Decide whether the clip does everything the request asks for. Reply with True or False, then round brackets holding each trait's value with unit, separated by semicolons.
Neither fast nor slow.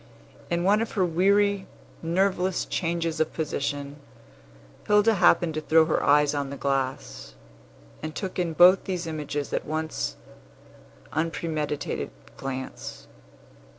False (120 wpm)